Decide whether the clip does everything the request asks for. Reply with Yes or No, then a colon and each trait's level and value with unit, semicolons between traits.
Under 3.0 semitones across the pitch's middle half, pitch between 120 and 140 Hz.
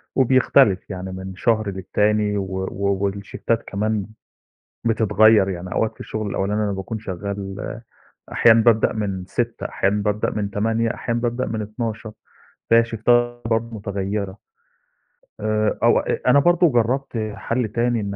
No: narrow, 2.5 semitones; low, 110 Hz